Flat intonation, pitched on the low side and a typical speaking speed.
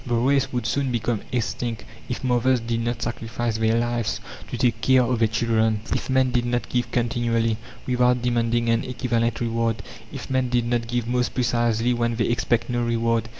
Yes: narrow, 1.2 semitones; low, 120 Hz; average, 190 wpm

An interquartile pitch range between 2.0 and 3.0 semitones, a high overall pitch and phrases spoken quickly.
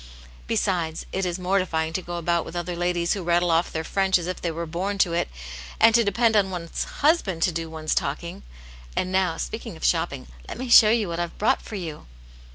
No: average, 2.7 semitones; medium, 175 Hz; fast, 225 wpm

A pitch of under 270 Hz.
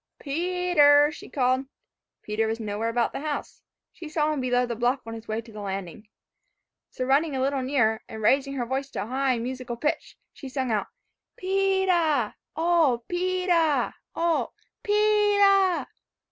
No: very high, 275 Hz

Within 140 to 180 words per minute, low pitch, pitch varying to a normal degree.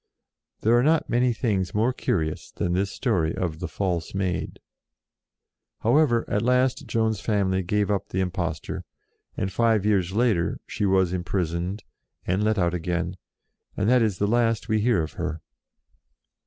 Yes: average, 170 wpm; low, 100 Hz; average, 4.3 semitones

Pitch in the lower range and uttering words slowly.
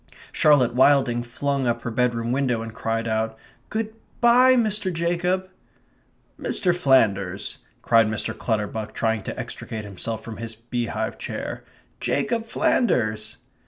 Yes: low, 120 Hz; slow, 125 wpm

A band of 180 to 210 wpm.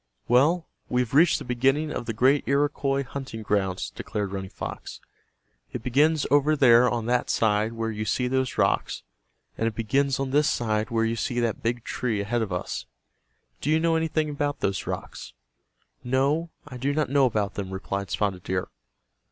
Yes: average, 185 wpm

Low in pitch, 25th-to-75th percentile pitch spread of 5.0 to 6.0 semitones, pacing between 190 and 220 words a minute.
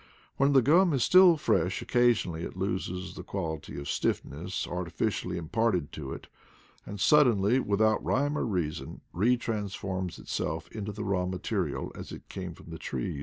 No: low, 100 Hz; wide, 5.4 semitones; average, 170 wpm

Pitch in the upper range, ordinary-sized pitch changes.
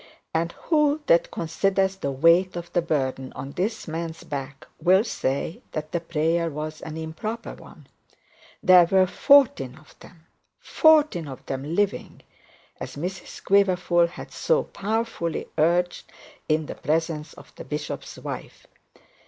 No: medium, 170 Hz; average, 3.6 semitones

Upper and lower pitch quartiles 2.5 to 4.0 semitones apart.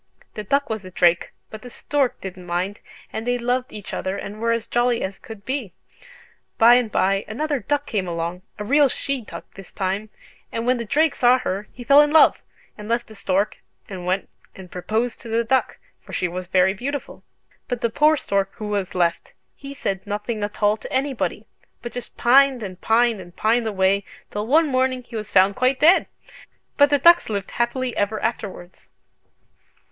No: average, 4.6 semitones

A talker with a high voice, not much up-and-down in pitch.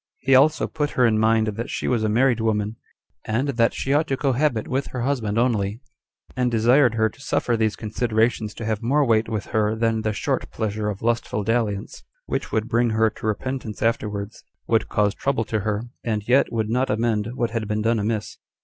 No: low, 115 Hz; narrow, 2.3 semitones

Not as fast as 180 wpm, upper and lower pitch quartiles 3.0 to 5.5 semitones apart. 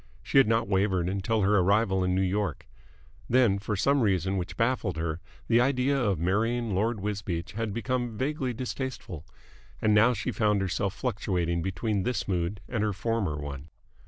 Yes: average, 170 wpm; average, 3.8 semitones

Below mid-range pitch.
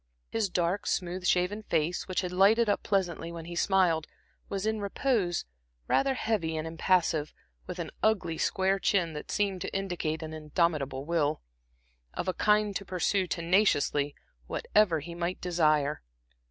No: medium, 180 Hz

